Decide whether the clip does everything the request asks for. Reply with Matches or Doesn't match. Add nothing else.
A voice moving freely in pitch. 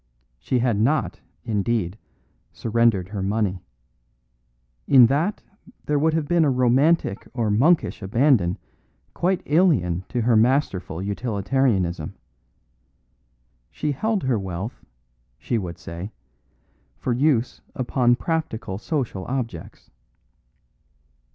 Matches